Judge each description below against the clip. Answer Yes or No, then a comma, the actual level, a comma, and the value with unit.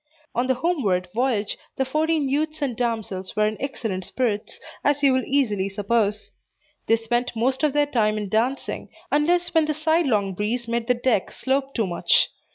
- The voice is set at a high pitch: Yes, high, 245 Hz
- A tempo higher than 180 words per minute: No, average, 175 wpm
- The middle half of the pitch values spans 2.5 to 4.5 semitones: No, average, 5.1 semitones